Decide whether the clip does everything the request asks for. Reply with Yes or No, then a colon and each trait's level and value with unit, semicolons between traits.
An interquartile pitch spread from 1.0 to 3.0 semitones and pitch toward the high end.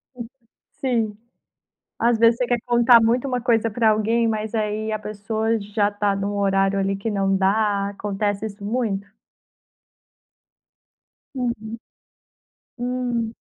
Yes: narrow, 2.4 semitones; high, 220 Hz